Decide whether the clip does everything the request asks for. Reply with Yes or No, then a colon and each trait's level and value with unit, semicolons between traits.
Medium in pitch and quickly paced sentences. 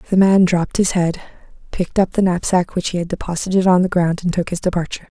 Yes: medium, 180 Hz; fast, 230 wpm